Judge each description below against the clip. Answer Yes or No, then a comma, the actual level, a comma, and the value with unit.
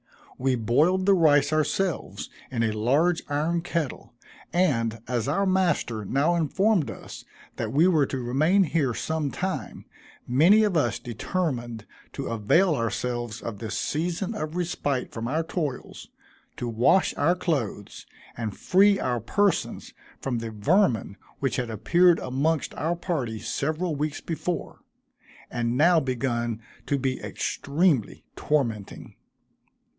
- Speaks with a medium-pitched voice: Yes, medium, 145 Hz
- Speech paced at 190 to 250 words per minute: No, slow, 135 wpm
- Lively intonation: Yes, wide, 6.3 semitones